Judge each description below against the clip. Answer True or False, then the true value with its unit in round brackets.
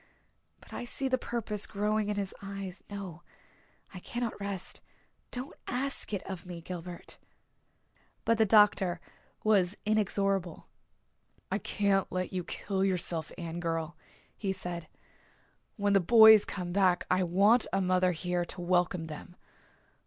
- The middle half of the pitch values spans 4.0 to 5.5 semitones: False (2.8 semitones)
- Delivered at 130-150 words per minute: True (140 wpm)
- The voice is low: False (190 Hz)